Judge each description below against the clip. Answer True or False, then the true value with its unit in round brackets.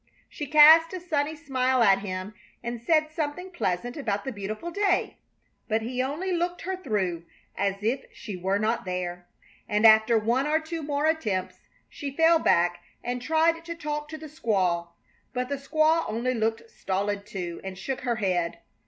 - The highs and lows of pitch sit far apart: True (7.5 semitones)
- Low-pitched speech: False (250 Hz)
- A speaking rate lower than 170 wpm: False (175 wpm)